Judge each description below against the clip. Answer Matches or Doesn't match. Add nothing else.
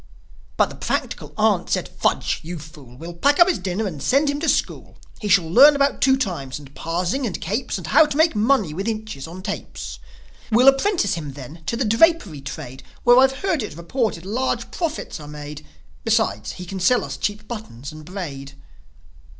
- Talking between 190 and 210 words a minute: Matches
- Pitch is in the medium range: Doesn't match